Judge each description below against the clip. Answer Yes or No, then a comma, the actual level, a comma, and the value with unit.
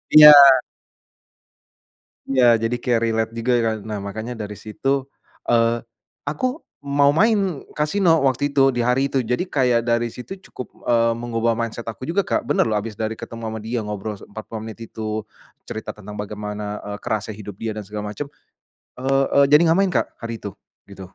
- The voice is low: Yes, low, 115 Hz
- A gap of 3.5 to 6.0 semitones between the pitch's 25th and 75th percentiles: Yes, average, 4.0 semitones